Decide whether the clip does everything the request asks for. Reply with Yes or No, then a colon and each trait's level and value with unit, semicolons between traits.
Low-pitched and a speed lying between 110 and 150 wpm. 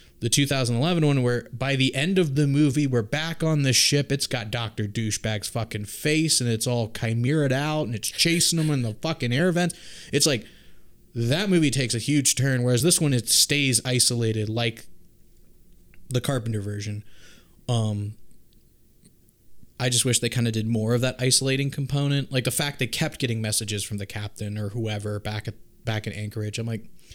No: low, 125 Hz; average, 190 wpm